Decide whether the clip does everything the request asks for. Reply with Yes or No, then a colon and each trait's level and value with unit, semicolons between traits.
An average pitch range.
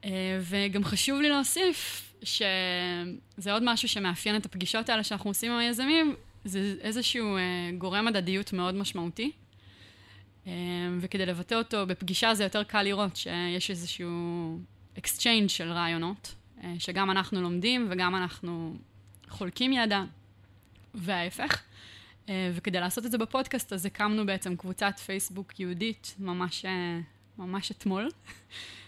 Yes: average, 3.1 semitones